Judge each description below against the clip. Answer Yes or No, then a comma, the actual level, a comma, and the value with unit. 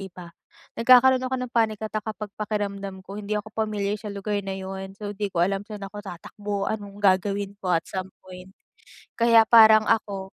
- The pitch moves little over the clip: Yes, narrow, 1.9 semitones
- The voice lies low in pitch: No, high, 205 Hz